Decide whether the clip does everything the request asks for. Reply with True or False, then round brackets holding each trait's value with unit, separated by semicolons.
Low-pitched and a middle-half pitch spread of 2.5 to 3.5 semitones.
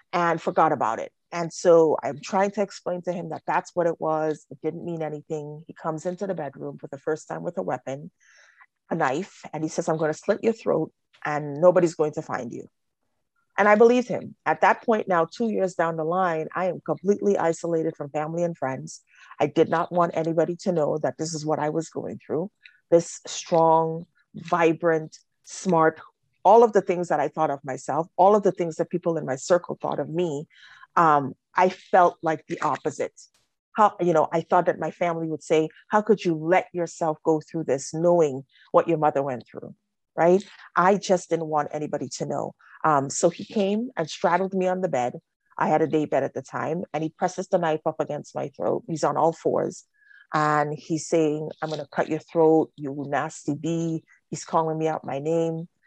False (165 Hz; 2.8 semitones)